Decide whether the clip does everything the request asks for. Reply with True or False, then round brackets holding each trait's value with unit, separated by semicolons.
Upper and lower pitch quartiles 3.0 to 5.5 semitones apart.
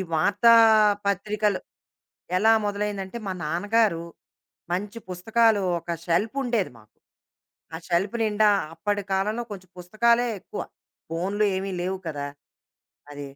True (3.3 semitones)